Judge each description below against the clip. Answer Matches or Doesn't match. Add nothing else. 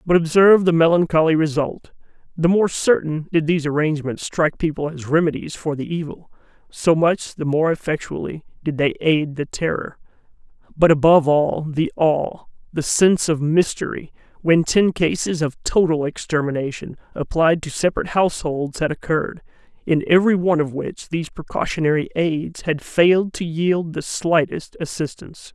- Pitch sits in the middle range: Matches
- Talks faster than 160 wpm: Doesn't match